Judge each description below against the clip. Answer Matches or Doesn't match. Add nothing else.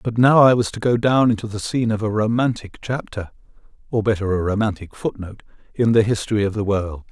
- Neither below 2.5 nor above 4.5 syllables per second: Doesn't match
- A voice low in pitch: Matches